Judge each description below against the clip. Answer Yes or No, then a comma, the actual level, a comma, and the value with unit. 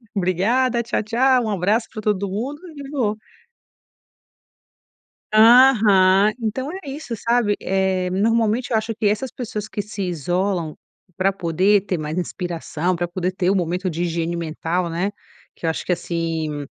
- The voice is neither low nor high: No, high, 195 Hz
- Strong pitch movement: No, average, 4.3 semitones